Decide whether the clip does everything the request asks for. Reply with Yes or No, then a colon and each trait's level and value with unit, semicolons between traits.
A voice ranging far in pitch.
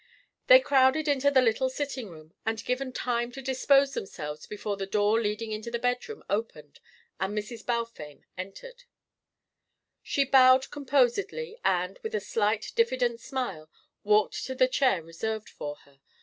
No: average, 4.4 semitones